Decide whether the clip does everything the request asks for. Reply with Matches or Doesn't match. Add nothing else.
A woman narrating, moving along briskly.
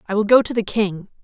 Matches